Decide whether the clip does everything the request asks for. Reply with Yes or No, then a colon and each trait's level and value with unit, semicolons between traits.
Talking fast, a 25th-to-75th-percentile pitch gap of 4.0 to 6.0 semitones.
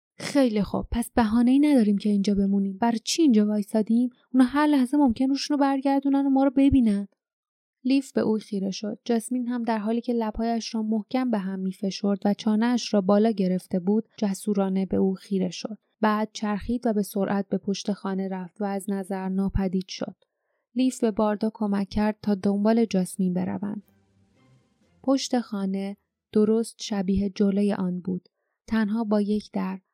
No: fast, 170 wpm; average, 3.3 semitones